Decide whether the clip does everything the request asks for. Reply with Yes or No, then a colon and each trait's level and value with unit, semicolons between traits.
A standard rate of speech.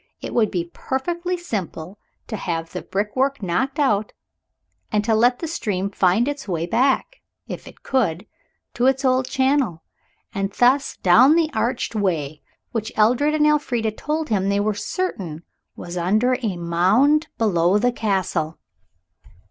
Yes: average, 150 wpm